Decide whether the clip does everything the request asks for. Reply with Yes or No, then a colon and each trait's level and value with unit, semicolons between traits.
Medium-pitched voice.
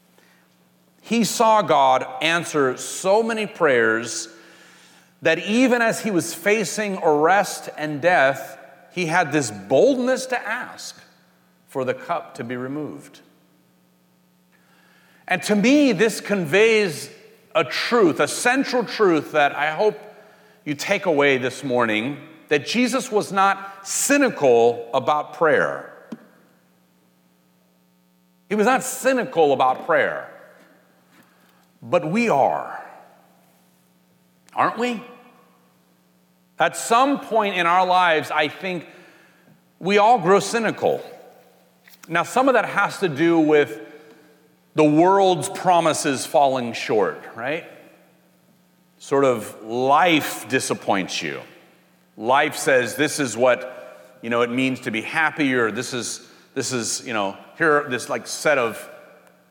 Yes: medium, 155 Hz